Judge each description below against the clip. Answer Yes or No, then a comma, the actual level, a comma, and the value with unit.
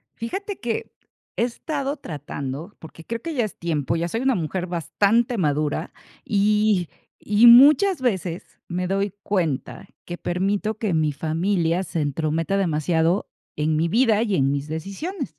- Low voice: No, medium, 185 Hz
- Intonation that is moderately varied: No, wide, 5.9 semitones